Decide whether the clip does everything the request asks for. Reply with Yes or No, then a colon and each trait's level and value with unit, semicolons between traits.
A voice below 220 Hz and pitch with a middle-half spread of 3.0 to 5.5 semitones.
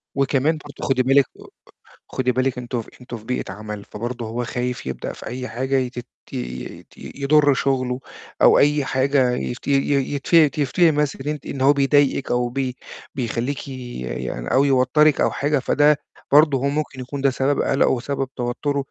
No: low, 135 Hz; narrow, 2.4 semitones